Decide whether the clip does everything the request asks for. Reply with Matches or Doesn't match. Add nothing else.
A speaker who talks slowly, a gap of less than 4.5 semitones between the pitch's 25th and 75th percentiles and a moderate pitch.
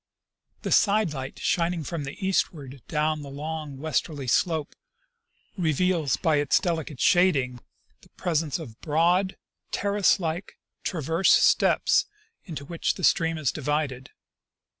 Matches